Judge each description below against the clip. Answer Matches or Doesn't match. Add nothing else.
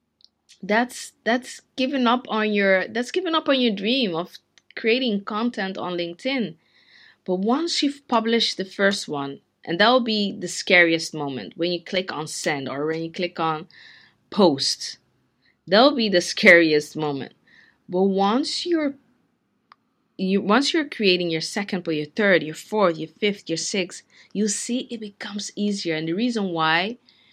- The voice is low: Doesn't match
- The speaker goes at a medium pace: Matches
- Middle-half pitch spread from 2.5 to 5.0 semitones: Doesn't match